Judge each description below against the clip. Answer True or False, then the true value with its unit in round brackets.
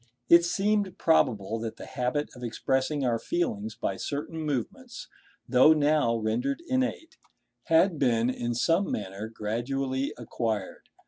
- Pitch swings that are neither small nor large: False (6.2 semitones)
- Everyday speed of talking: False (130 wpm)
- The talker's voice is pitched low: True (130 Hz)